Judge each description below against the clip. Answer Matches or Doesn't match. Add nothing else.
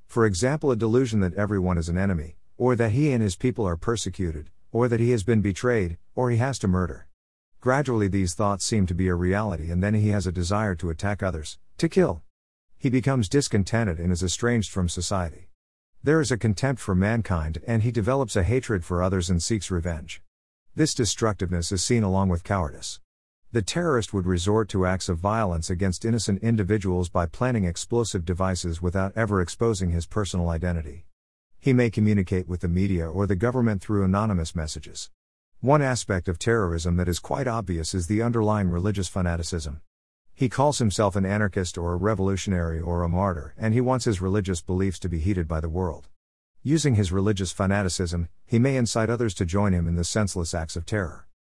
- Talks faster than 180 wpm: Matches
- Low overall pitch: Matches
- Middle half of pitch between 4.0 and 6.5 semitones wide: Matches